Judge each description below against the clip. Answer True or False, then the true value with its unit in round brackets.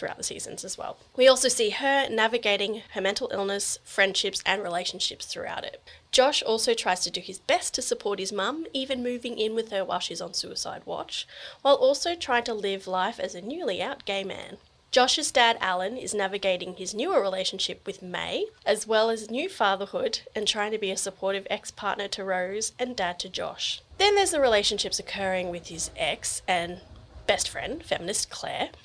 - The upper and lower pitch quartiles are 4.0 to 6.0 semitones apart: True (4.3 semitones)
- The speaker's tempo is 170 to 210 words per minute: True (195 wpm)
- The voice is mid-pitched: False (205 Hz)